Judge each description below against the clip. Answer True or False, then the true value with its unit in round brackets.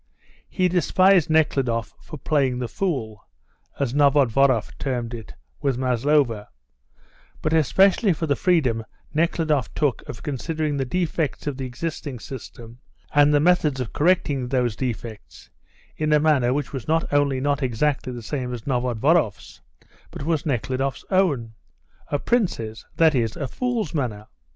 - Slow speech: False (145 wpm)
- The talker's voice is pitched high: False (140 Hz)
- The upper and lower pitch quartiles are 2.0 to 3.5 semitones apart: False (4.3 semitones)